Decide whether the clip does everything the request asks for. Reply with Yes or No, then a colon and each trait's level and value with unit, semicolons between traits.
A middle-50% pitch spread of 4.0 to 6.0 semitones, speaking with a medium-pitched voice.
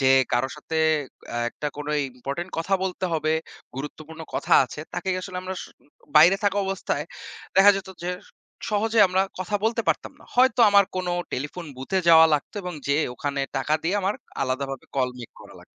Yes: average, 5.3 semitones; medium, 165 Hz